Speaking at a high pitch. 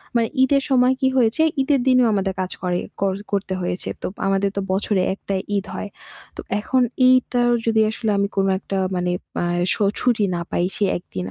Yes: high, 205 Hz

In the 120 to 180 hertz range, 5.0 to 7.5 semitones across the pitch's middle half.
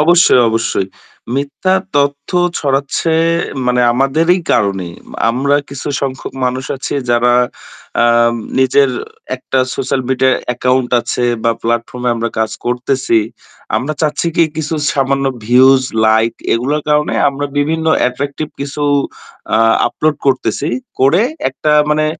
No: low, 135 Hz; average, 2.8 semitones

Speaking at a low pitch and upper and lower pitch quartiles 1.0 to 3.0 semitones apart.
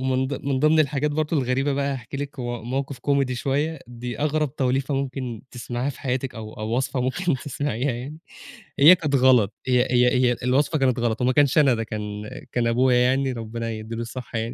Yes: low, 130 Hz; narrow, 2.6 semitones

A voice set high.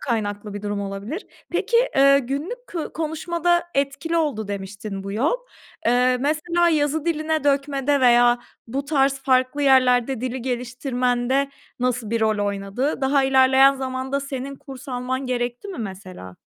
Yes: very high, 265 Hz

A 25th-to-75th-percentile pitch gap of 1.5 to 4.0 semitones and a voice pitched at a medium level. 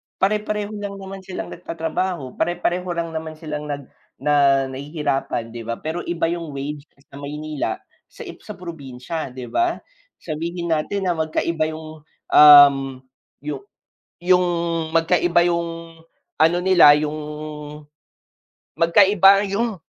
Yes: average, 3.2 semitones; medium, 165 Hz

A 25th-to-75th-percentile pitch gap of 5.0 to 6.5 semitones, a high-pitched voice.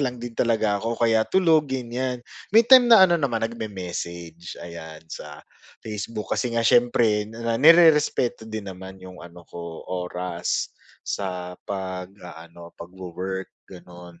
No: average, 5.3 semitones; low, 105 Hz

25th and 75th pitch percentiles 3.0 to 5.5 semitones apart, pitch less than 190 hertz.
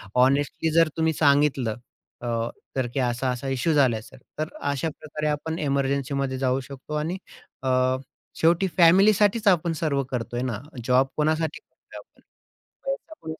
Yes: average, 3.7 semitones; medium, 140 Hz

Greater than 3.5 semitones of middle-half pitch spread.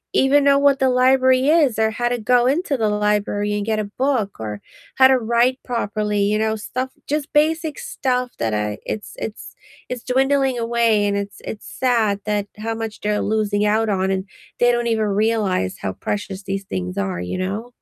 Yes: average, 3.9 semitones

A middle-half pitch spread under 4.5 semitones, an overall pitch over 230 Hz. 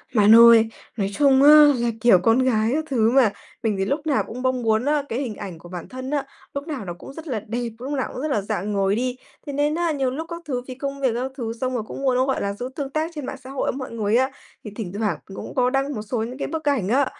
Yes: average, 4.0 semitones; very high, 255 Hz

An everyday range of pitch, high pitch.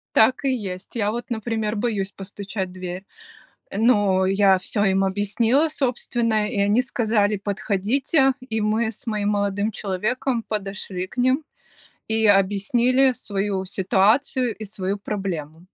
Yes: average, 3.1 semitones; high, 210 Hz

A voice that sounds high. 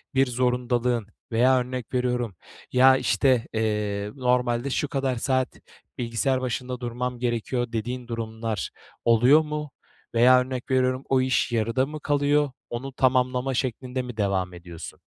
No: low, 125 Hz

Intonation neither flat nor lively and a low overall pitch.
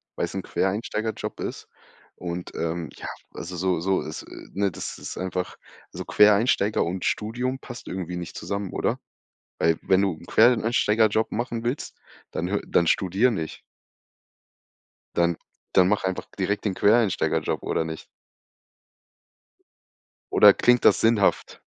Yes: average, 3.8 semitones; low, 100 Hz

